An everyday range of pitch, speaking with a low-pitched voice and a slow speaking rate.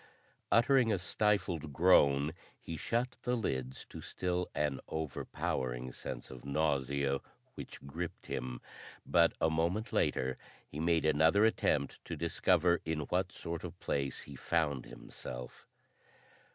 Yes: average, 4.3 semitones; very low, 80 Hz; slow, 130 wpm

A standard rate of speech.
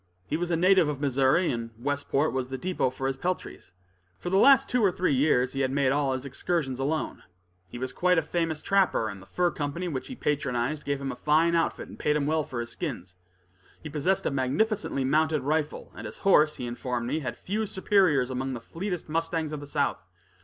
No: fast, 220 wpm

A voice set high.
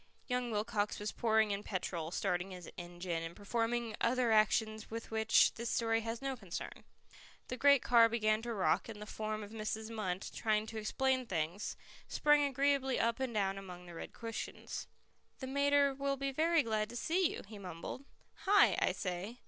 Yes: high, 220 Hz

